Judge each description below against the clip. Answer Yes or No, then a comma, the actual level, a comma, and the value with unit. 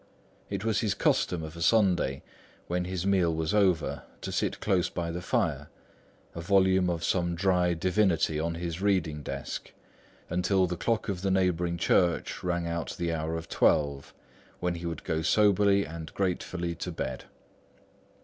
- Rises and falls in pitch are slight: Yes, narrow, 2.3 semitones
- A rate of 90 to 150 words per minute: No, average, 165 wpm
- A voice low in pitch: Yes, very low, 85 Hz